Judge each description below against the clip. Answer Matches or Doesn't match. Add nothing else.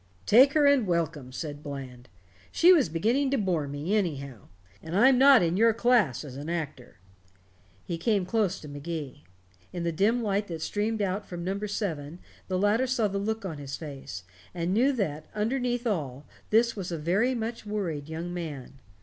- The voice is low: Doesn't match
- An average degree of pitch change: Doesn't match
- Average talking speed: Matches